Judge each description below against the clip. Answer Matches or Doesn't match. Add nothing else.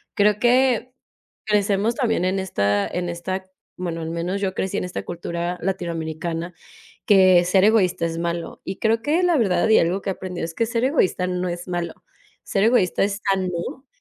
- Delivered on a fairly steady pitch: Doesn't match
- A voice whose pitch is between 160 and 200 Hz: Matches